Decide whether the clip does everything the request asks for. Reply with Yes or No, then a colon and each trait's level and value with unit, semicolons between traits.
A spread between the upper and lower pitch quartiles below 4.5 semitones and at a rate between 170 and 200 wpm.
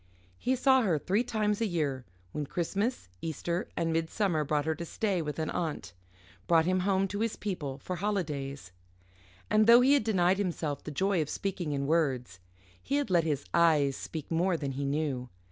No: average, 5.2 semitones; average, 190 wpm